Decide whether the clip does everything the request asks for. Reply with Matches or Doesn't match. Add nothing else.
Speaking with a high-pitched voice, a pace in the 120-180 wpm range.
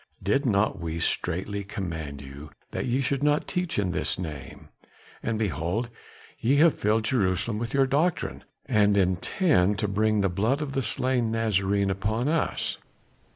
Doesn't match